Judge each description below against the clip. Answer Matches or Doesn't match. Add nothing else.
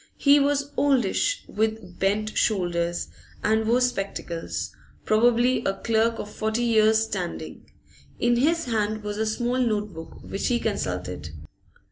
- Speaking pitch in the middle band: Doesn't match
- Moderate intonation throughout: Matches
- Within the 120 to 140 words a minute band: Matches